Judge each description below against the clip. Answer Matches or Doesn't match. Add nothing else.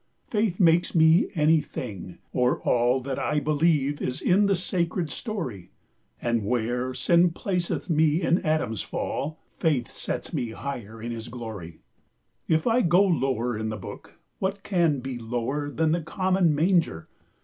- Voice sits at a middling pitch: Matches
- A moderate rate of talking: Matches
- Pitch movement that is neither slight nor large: Doesn't match